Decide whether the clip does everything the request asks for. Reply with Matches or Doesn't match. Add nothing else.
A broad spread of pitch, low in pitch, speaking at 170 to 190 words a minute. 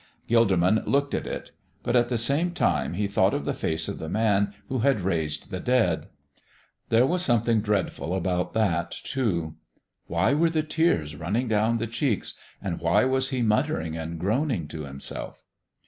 Matches